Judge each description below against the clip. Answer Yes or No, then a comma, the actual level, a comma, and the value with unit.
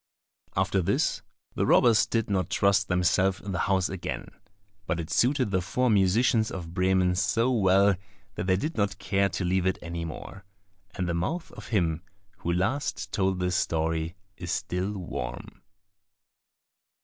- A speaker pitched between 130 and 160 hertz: No, very low, 95 Hz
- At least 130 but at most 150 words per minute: No, average, 160 wpm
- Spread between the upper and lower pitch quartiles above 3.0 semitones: No, narrow, 2.4 semitones